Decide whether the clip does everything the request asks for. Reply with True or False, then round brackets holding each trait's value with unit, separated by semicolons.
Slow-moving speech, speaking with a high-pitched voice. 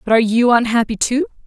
False (205 wpm; 230 Hz)